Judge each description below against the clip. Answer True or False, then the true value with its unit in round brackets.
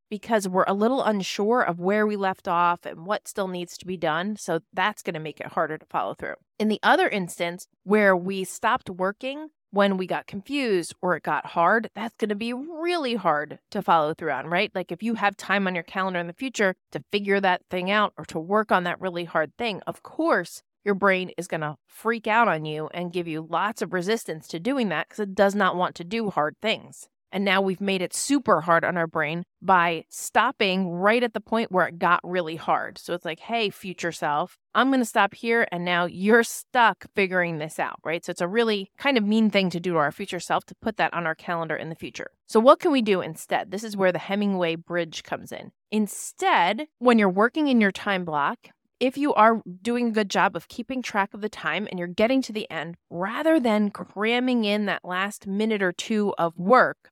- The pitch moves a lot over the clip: False (4.0 semitones)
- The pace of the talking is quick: True (235 wpm)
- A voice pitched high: True (195 Hz)